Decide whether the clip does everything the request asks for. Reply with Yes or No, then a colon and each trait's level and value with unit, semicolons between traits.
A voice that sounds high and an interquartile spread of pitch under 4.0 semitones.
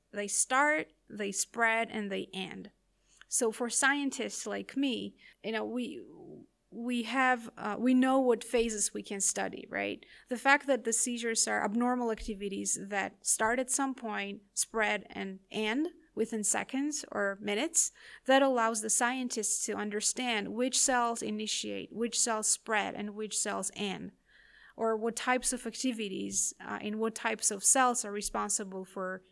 Yes: high, 225 Hz; average, 3.3 semitones